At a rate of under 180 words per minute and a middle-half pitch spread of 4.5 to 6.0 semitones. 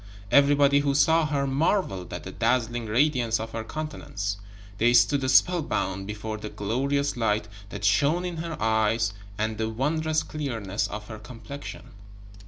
Yes: average, 150 wpm; average, 5.0 semitones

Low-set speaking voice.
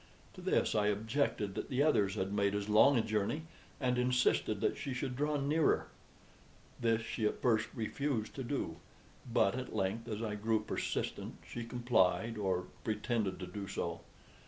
Yes: low, 110 Hz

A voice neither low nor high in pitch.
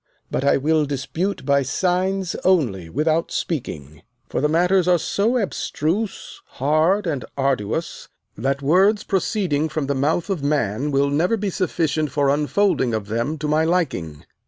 Yes: medium, 155 Hz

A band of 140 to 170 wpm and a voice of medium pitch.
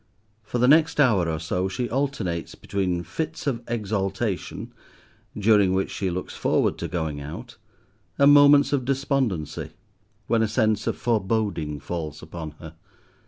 No: average, 145 wpm; low, 100 Hz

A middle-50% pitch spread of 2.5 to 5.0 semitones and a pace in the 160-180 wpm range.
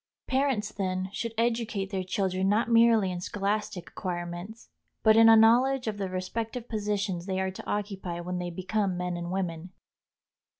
Yes: average, 3.4 semitones; average, 165 wpm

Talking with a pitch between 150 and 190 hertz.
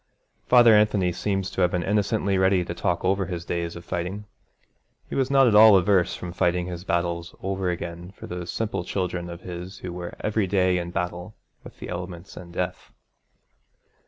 No: very low, 90 Hz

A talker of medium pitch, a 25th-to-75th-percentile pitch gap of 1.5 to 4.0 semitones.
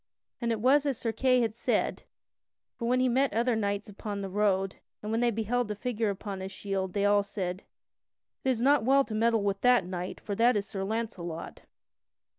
No: high, 215 Hz; average, 3.4 semitones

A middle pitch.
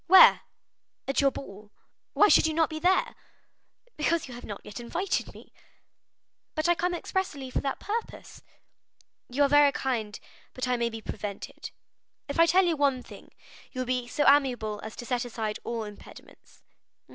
No: very high, 270 Hz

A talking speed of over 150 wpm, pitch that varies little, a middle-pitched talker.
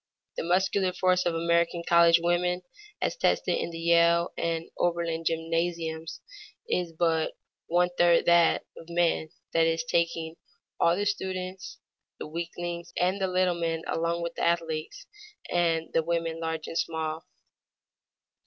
No: average, 145 wpm; narrow, 1.1 semitones; medium, 170 Hz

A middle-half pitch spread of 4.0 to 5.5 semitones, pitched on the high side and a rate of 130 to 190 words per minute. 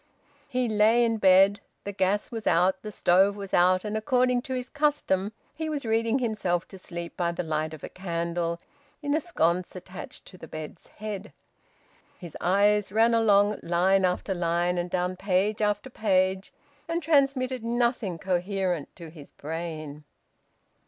Yes: average, 4.3 semitones; high, 195 Hz; average, 160 wpm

